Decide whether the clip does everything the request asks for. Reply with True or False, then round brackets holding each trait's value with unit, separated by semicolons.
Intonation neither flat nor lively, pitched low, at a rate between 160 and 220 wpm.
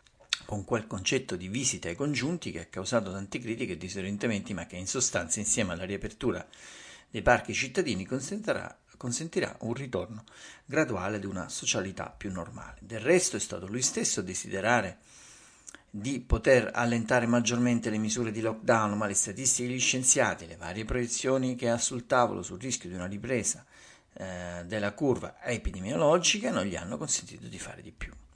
True (4.4 semitones; 110 Hz; 165 wpm)